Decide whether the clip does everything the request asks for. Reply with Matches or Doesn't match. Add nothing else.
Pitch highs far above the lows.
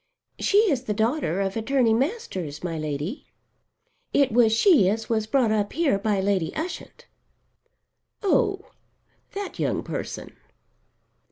Matches